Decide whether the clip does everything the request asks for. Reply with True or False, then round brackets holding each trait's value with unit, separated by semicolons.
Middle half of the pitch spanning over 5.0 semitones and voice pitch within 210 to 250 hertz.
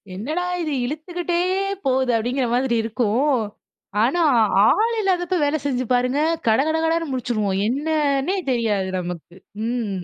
False (5.4 semitones; 265 Hz)